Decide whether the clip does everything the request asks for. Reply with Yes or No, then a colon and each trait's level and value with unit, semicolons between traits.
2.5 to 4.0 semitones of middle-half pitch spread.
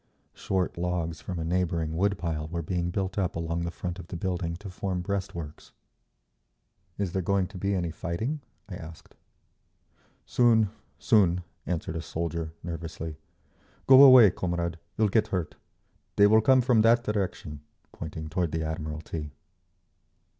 Yes: average, 3.3 semitones